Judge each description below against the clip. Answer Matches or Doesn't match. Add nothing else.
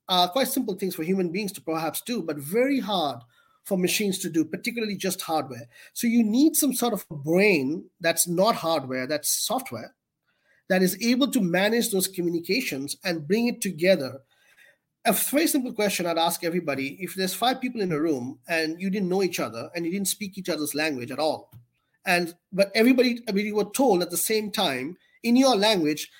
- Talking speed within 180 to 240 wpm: Matches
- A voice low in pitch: Doesn't match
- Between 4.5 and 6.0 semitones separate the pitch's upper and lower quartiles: Matches